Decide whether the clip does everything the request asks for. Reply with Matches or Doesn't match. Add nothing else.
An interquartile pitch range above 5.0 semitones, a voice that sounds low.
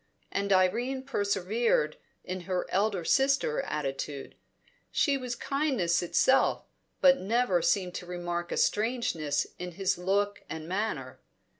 Doesn't match